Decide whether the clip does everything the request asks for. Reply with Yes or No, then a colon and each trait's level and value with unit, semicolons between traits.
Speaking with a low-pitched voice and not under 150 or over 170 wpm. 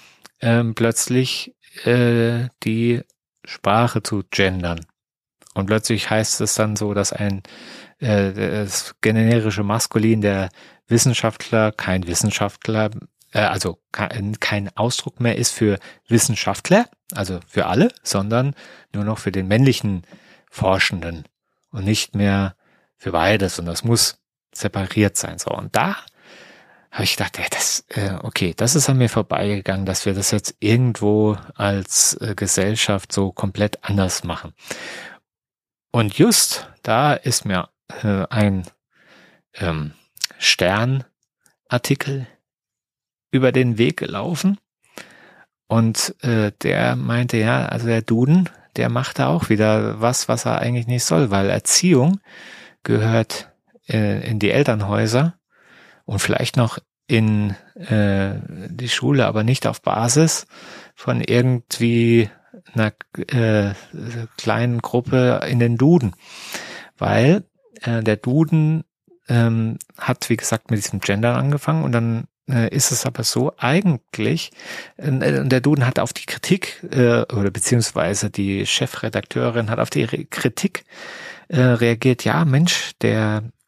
No: low, 115 Hz; slow, 125 wpm